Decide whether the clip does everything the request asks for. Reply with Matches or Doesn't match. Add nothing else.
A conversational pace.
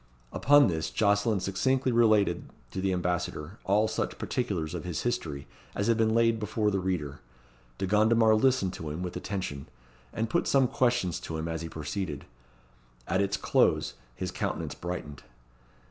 Matches